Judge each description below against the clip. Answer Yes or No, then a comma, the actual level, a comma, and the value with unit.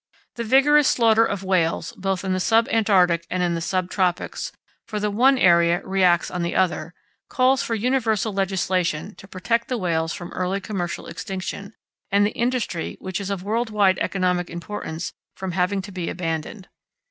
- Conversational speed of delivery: Yes, average, 175 wpm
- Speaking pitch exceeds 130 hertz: Yes, high, 190 Hz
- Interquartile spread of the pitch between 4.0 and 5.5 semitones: No, average, 3.5 semitones